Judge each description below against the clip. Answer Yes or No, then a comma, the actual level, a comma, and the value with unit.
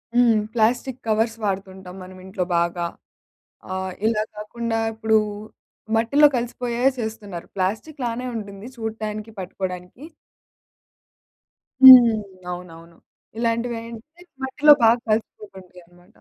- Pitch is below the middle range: No, high, 220 Hz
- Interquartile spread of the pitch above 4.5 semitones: No, average, 3.9 semitones